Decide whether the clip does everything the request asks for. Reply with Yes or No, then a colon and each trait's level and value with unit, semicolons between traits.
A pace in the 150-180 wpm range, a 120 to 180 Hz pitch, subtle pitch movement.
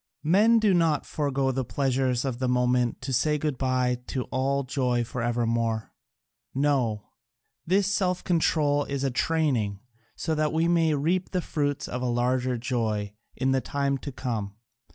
No: average, 165 wpm; low, 135 Hz; average, 3.7 semitones